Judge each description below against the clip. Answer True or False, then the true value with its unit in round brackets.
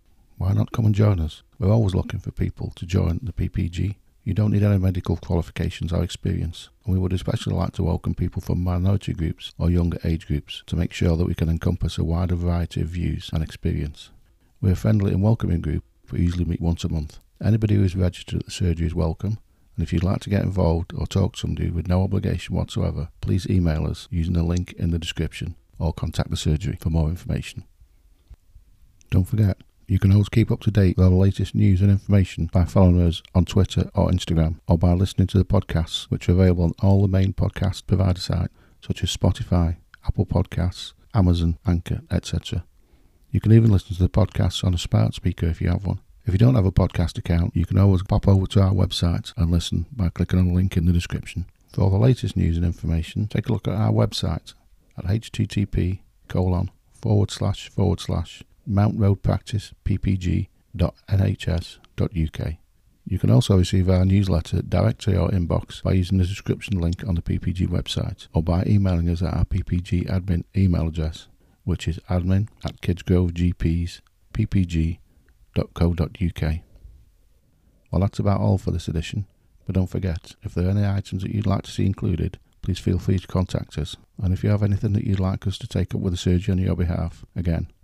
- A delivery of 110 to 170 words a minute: False (200 wpm)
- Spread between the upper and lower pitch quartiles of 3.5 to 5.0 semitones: False (2.9 semitones)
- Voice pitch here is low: True (95 Hz)